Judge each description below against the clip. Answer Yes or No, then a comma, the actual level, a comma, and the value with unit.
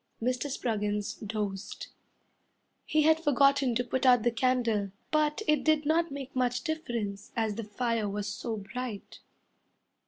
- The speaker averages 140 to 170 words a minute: Yes, average, 145 wpm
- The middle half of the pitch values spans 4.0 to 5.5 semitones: Yes, average, 4.7 semitones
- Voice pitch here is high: Yes, high, 245 Hz